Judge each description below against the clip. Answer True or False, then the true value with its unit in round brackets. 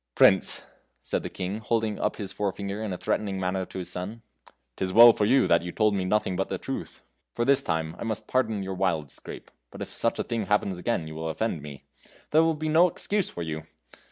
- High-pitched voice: False (100 Hz)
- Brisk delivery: True (230 wpm)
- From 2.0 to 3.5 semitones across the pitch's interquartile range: False (4.0 semitones)